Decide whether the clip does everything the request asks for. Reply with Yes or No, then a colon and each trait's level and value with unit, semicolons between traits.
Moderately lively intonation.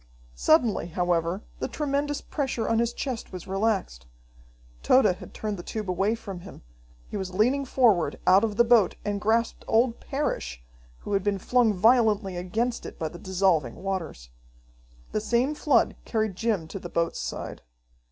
Yes: average, 4.6 semitones